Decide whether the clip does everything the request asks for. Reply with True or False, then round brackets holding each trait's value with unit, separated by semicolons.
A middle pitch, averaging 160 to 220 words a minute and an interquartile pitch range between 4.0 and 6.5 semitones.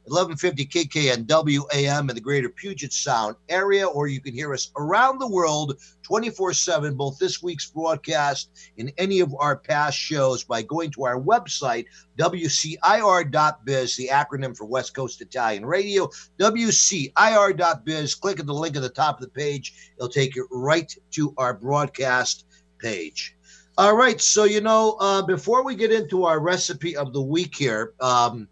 True (150 Hz; 165 wpm; 5.4 semitones)